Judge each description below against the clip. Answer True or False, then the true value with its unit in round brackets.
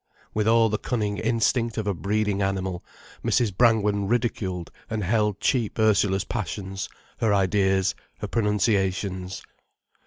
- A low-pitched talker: True (105 Hz)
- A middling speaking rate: False (125 wpm)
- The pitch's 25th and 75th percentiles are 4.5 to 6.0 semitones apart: False (2.5 semitones)